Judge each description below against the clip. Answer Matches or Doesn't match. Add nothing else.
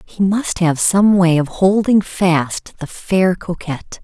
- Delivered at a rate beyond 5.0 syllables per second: Doesn't match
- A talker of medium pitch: Matches